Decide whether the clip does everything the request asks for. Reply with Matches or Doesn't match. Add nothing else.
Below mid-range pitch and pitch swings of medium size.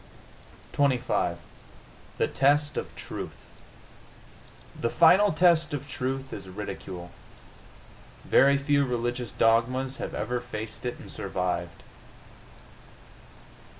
Matches